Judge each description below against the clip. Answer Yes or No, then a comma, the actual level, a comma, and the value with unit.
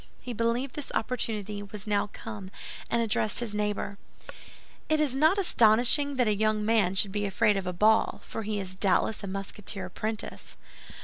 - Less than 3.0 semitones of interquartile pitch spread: Yes, narrow, 2.5 semitones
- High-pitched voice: Yes, high, 215 Hz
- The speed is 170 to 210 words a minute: Yes, average, 175 wpm